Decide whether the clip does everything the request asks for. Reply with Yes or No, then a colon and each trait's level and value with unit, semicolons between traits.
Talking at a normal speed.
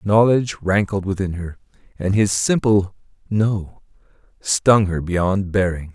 No: slow, 130 wpm